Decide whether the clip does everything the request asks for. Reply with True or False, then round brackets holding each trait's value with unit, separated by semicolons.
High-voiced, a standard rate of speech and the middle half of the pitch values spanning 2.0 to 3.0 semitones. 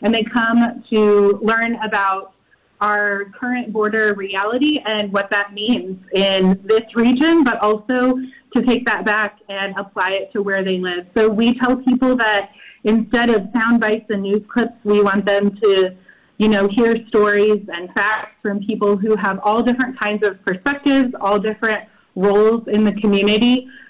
True (215 Hz; 170 wpm; 2.5 semitones)